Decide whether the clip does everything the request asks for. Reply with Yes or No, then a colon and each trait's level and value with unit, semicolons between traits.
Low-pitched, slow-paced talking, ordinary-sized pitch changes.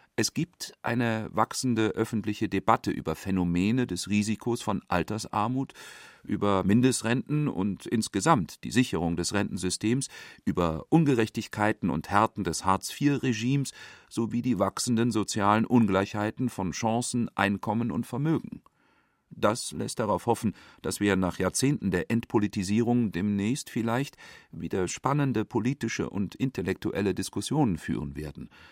Yes: low, 110 Hz; slow, 115 wpm; average, 3.3 semitones